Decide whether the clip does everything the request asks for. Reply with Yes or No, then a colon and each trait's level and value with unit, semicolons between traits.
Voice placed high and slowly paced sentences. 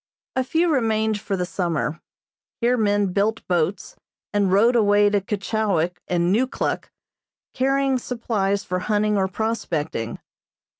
Yes: high, 205 Hz; slow, 130 wpm